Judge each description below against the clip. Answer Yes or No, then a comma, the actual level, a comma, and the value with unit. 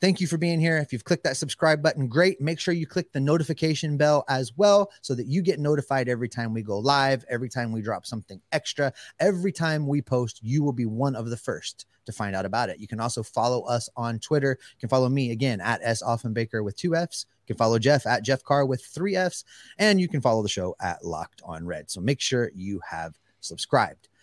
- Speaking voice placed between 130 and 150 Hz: Yes, low, 135 Hz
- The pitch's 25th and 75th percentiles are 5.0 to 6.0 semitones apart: Yes, average, 5.3 semitones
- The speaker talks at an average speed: No, fast, 240 wpm